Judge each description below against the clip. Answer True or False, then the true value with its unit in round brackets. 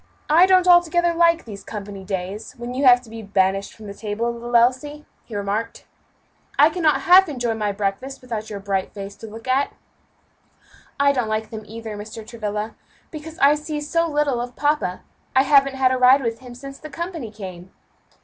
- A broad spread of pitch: True (5.7 semitones)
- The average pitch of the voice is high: True (240 Hz)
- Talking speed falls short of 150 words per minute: False (190 wpm)